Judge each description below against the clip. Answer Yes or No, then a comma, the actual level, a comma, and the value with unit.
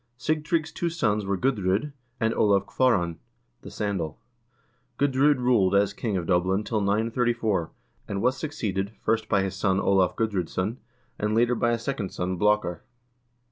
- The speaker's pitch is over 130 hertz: No, low, 105 Hz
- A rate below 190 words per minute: Yes, average, 155 wpm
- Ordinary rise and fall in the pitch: Yes, average, 4.2 semitones